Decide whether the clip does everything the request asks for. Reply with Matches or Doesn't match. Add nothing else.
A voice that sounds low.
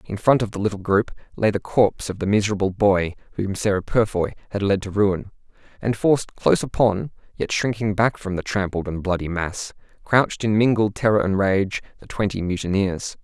Matches